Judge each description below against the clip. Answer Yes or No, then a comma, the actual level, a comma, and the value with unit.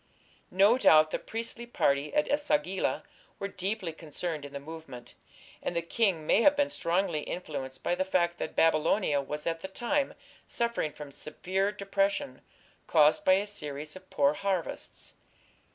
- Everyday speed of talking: Yes, average, 160 wpm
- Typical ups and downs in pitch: Yes, average, 4.9 semitones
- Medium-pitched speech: Yes, medium, 175 Hz